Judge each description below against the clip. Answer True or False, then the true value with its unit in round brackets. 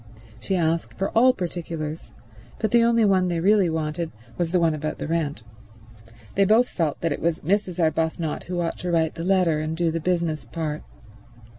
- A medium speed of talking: True (190 wpm)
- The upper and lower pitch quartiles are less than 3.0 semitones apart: True (2.5 semitones)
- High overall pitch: False (170 Hz)